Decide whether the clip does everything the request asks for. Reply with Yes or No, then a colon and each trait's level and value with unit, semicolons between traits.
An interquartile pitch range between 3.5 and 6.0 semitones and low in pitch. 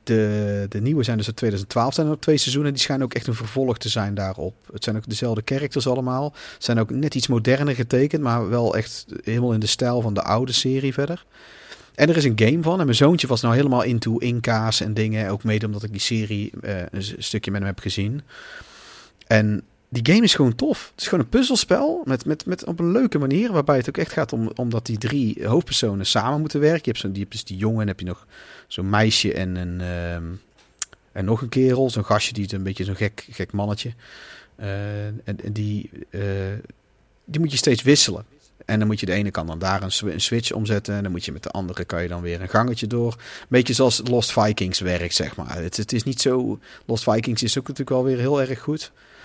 Yes: average, 4.3 semitones; low, 115 Hz